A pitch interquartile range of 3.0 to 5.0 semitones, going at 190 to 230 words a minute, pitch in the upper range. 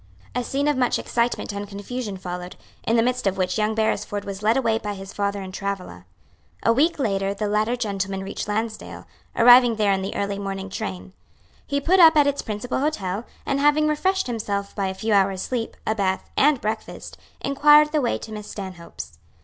Yes: average, 4.2 semitones; average, 200 wpm; high, 215 Hz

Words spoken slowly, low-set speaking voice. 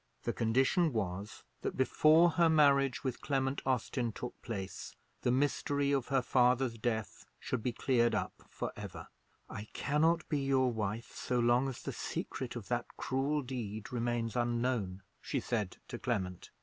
No: average, 160 wpm; low, 125 Hz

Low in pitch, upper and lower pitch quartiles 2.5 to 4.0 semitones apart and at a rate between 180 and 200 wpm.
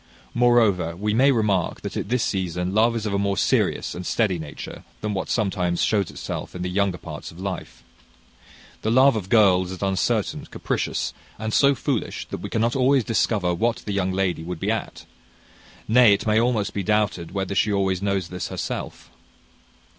Yes: low, 100 Hz; average, 3.5 semitones; average, 185 wpm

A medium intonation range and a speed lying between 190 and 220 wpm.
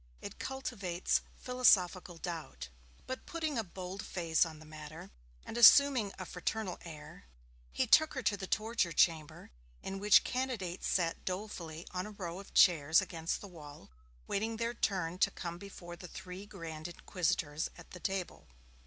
No: average, 4.2 semitones; average, 160 wpm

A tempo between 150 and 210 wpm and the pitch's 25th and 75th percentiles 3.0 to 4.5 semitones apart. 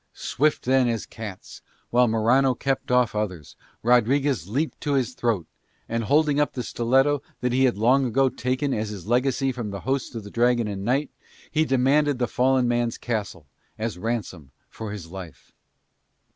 Yes: average, 170 wpm; average, 3.5 semitones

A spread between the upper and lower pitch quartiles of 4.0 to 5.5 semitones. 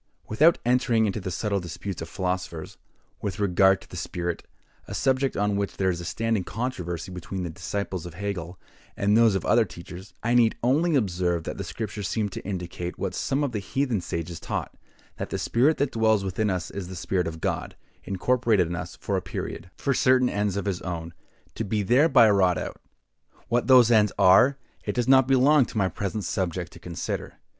Yes: average, 4.7 semitones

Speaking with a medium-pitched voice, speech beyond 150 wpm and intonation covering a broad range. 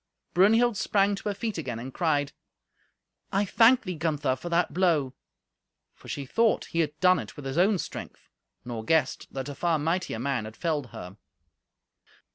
Yes: medium, 160 Hz; average, 175 wpm; wide, 5.8 semitones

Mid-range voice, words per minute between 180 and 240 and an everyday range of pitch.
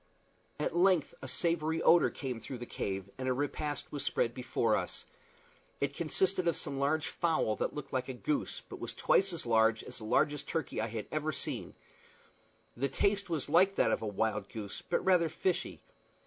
No: medium, 145 Hz; average, 195 wpm; wide, 6.1 semitones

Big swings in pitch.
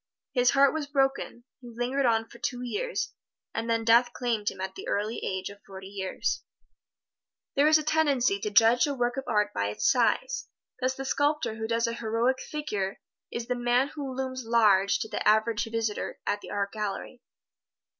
No: average, 3.8 semitones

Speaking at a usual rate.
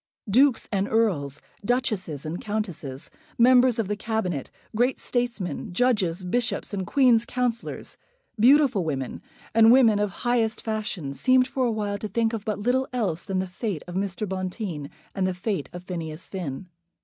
Yes: average, 160 wpm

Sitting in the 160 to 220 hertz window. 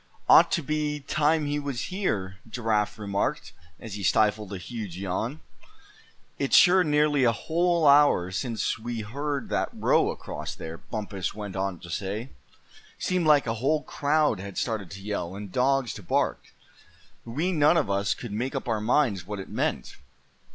No: low, 115 Hz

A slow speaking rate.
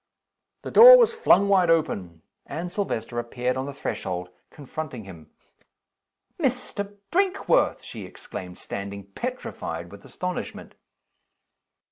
Yes: slow, 110 wpm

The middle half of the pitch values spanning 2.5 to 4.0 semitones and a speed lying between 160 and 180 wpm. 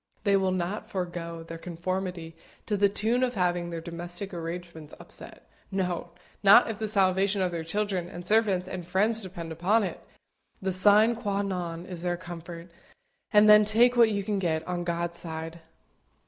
Yes: average, 2.9 semitones; average, 175 wpm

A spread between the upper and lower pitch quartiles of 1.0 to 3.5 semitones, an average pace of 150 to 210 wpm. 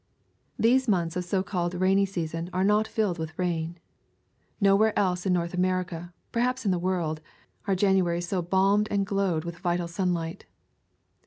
Yes: narrow, 2.4 semitones; average, 160 wpm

